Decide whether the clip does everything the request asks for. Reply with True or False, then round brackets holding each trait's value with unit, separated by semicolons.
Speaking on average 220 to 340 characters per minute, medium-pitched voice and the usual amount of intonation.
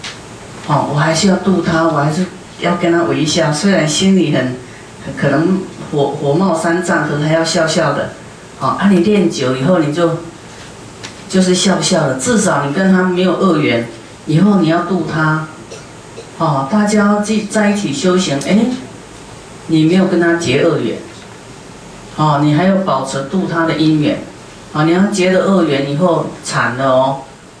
True (235 characters per minute; 165 Hz; 3.9 semitones)